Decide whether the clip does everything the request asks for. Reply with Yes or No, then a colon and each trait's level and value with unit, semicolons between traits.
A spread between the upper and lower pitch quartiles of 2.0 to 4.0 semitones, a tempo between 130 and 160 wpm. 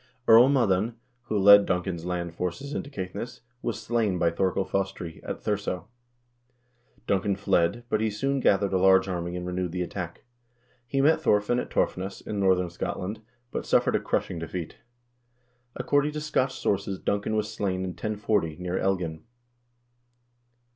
Yes: average, 3.2 semitones; average, 155 wpm